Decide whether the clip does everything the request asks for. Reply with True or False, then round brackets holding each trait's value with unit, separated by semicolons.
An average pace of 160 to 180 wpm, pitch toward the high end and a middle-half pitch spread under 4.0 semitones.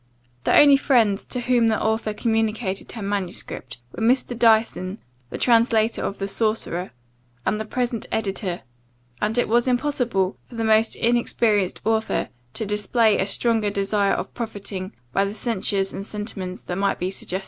True (165 wpm; 215 Hz; 2.9 semitones)